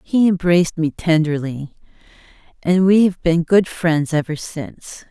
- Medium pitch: Yes, medium, 165 Hz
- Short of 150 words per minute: Yes, average, 140 wpm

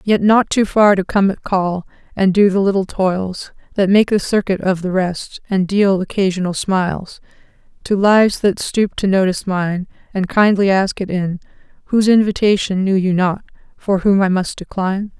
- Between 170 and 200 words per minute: Yes, average, 180 wpm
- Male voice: No, female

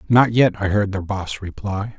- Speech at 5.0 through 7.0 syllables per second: No, 4.4 syllables/s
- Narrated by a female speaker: No, male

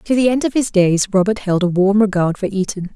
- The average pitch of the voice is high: Yes, high, 200 Hz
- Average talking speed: No, fast, 265 wpm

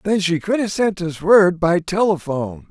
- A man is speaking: Yes, male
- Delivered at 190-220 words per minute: Yes, average, 200 wpm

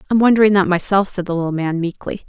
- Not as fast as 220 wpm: No, fast, 235 wpm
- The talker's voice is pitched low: No, high, 190 Hz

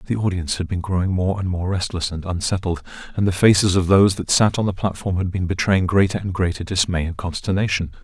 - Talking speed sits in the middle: No, fast, 225 wpm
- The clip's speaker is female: No, male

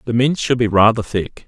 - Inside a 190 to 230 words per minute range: No, fast, 245 wpm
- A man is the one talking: Yes, male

